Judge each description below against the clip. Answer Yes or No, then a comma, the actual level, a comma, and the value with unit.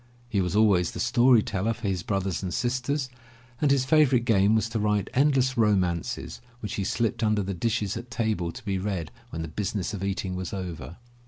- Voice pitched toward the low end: Yes, low, 105 Hz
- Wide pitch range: No, average, 4.3 semitones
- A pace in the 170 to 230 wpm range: Yes, average, 200 wpm